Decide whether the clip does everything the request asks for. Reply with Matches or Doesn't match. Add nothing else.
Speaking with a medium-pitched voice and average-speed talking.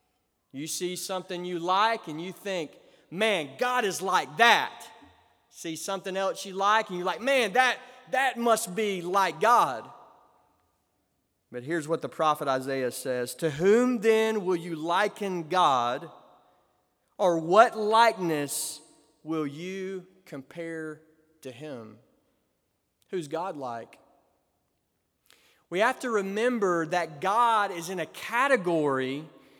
Doesn't match